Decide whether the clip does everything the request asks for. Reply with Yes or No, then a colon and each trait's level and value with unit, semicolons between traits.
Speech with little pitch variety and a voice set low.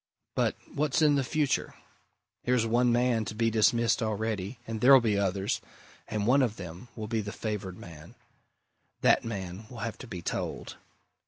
No: average, 3.3 semitones; low, 110 Hz